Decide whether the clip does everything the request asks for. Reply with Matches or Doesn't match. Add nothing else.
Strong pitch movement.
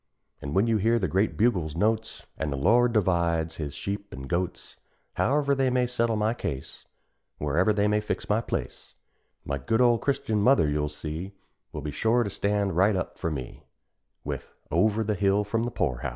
Matches